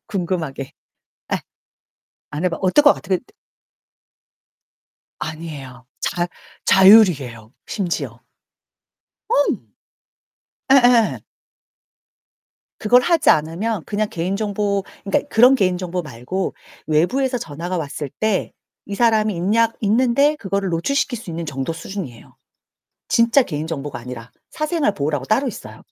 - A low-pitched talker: No, high, 190 Hz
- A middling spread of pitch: No, wide, 6.3 semitones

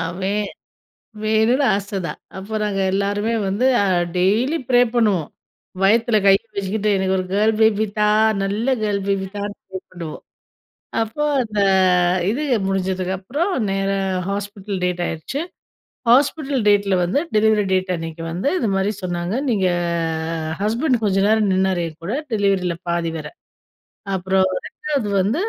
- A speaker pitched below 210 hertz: Yes, high, 200 Hz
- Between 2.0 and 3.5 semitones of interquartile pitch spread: Yes, narrow, 2.6 semitones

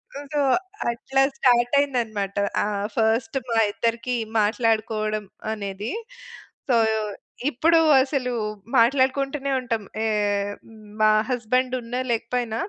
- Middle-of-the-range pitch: No, high, 235 Hz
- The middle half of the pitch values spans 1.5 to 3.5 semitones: Yes, average, 3.1 semitones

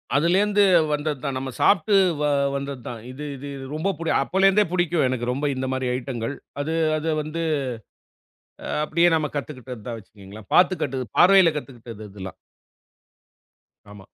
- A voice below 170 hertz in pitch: Yes, medium, 140 Hz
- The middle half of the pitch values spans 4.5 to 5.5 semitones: Yes, average, 5.0 semitones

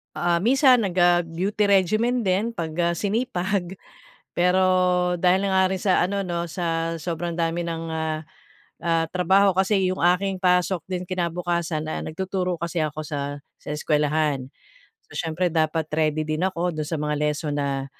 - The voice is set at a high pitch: No, medium, 175 Hz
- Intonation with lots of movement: No, average, 3.0 semitones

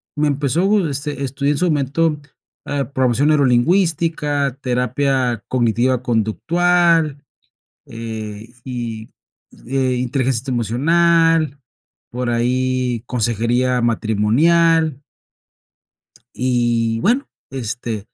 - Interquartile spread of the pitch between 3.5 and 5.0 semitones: Yes, average, 4.1 semitones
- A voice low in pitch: Yes, low, 130 Hz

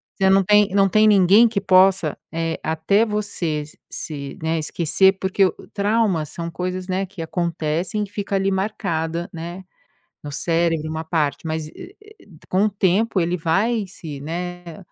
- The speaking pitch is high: No, medium, 180 Hz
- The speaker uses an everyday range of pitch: Yes, average, 3.4 semitones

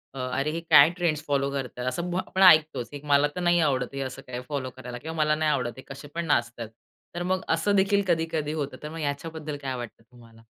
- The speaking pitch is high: No, medium, 145 Hz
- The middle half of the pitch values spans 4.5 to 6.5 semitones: No, average, 4.0 semitones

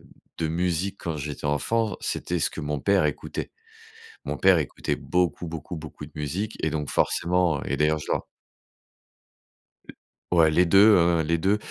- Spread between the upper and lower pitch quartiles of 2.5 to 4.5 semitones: Yes, average, 2.9 semitones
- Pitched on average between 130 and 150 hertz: No, very low, 85 Hz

